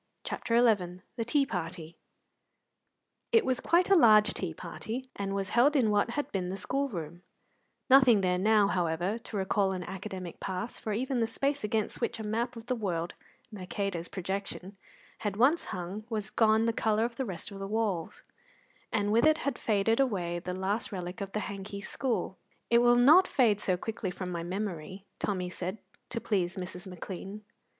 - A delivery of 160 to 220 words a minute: Yes, average, 185 wpm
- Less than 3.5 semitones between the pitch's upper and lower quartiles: No, average, 4.1 semitones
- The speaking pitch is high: Yes, high, 205 Hz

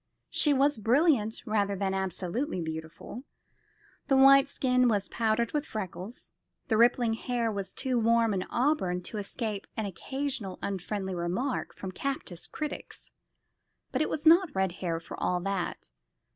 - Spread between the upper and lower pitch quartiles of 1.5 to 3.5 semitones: No, wide, 5.6 semitones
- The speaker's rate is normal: Yes, average, 145 wpm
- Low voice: No, high, 220 Hz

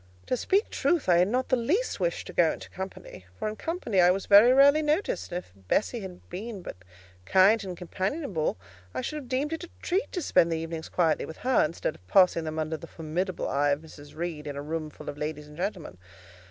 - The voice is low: No, medium, 180 Hz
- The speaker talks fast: Yes, fast, 230 wpm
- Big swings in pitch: Yes, wide, 8.1 semitones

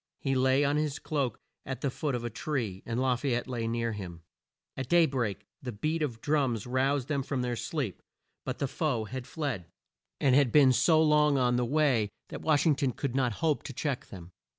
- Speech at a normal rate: No, fast, 220 wpm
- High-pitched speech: No, low, 130 Hz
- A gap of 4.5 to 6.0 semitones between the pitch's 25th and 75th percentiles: No, average, 3.6 semitones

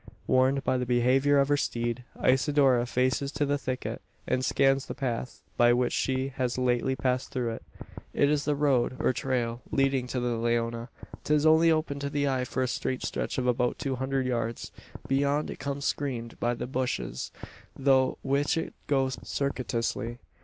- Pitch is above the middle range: No, low, 130 Hz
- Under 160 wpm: No, average, 180 wpm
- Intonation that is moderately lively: No, narrow, 2.3 semitones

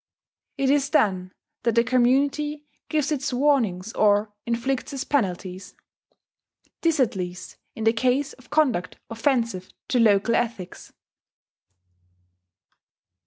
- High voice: Yes, high, 240 Hz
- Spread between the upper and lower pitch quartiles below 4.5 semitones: No, average, 5.1 semitones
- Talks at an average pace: No, slow, 115 wpm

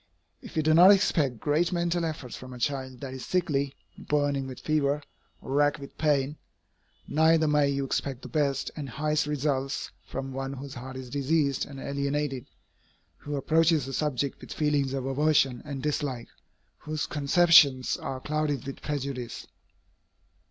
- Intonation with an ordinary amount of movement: No, narrow, 2.2 semitones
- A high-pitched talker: No, medium, 140 Hz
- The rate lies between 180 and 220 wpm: No, average, 160 wpm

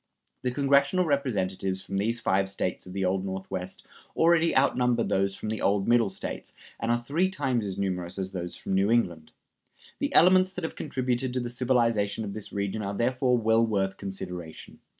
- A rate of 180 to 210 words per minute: Yes, average, 185 wpm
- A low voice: Yes, low, 110 Hz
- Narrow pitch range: No, average, 4.8 semitones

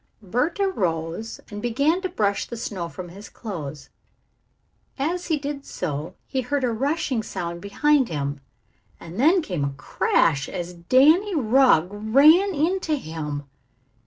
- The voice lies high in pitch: Yes, high, 225 Hz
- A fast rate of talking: No, average, 140 wpm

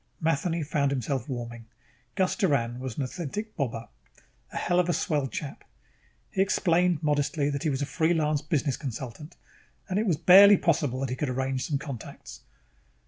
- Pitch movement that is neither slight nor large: Yes, average, 4.3 semitones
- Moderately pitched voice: Yes, medium, 145 Hz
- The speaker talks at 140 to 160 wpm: No, average, 175 wpm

